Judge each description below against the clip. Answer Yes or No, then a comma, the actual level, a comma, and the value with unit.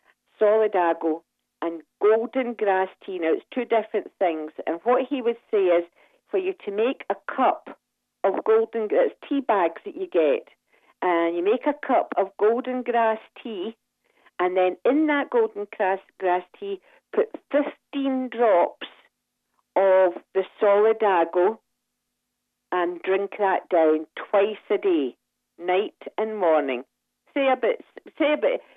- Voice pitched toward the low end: No, high, 220 Hz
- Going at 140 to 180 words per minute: Yes, average, 145 wpm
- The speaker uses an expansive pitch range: Yes, wide, 8.3 semitones